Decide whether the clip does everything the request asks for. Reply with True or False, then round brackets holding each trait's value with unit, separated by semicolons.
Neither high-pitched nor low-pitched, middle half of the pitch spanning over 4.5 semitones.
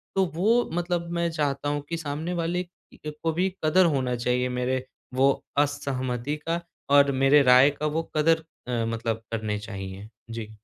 True (145 Hz; 4.9 semitones)